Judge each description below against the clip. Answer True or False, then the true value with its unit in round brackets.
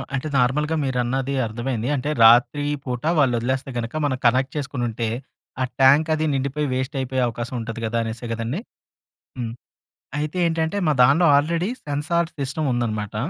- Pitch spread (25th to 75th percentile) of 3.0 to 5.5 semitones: True (3.6 semitones)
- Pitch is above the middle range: False (130 Hz)